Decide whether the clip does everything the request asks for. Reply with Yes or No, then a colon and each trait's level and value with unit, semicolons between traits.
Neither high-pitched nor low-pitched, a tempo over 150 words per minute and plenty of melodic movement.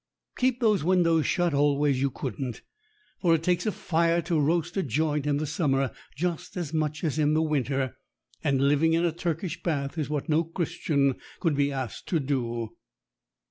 No: medium, 155 Hz; average, 180 wpm; average, 3.3 semitones